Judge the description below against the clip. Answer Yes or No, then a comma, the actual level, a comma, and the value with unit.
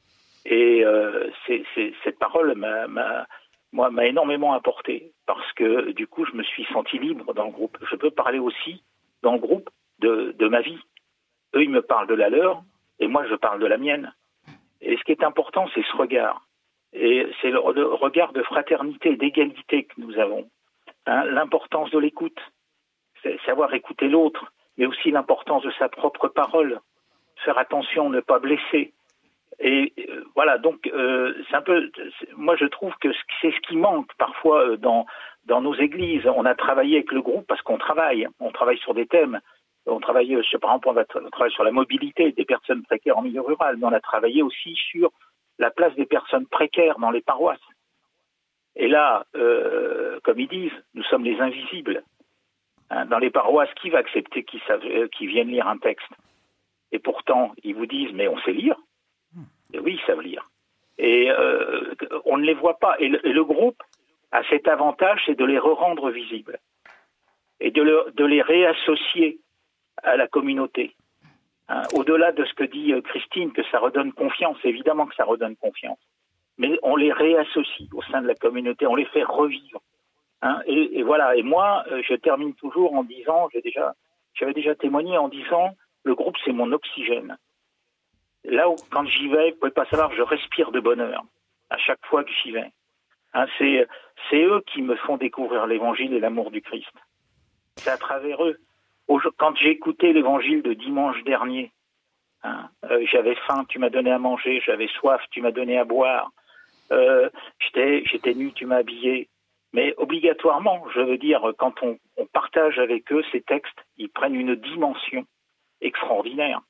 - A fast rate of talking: No, average, 190 wpm